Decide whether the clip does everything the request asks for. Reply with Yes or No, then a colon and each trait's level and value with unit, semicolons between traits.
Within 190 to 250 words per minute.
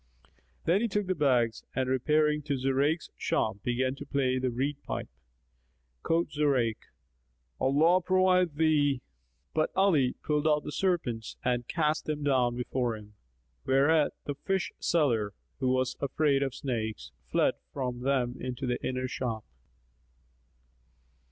No: slow, 135 wpm